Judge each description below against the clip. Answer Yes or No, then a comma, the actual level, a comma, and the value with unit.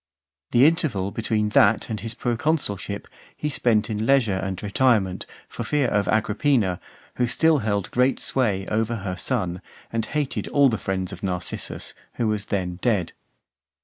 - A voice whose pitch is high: No, low, 110 Hz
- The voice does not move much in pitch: No, average, 4.3 semitones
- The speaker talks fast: No, average, 155 wpm